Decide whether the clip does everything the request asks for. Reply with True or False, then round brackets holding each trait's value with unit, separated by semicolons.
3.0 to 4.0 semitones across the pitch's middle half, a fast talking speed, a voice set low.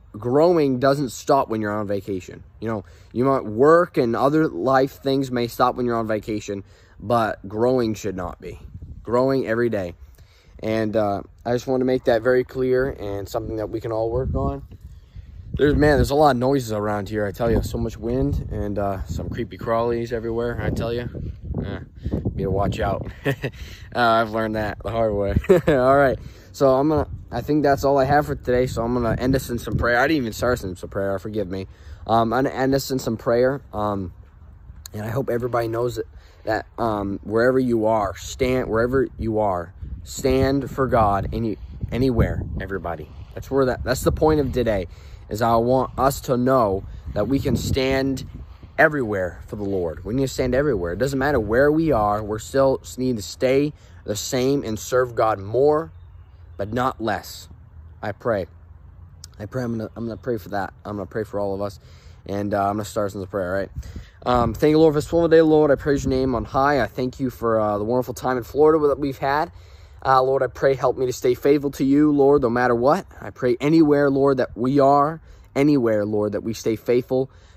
False (4.8 semitones; 215 wpm; 115 Hz)